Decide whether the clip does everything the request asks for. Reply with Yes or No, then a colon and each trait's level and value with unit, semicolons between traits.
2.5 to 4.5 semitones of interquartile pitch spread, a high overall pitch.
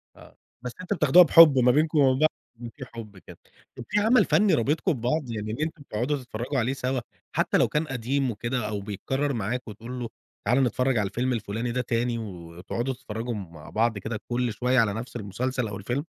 No: average, 3.4 semitones; low, 120 Hz